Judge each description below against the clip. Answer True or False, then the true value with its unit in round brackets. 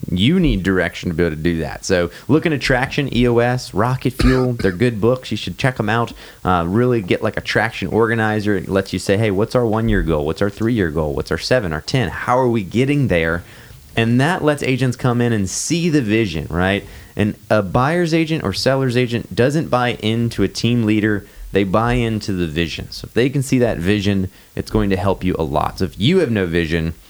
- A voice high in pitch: False (110 Hz)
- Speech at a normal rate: False (235 wpm)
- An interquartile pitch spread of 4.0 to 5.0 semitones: True (4.4 semitones)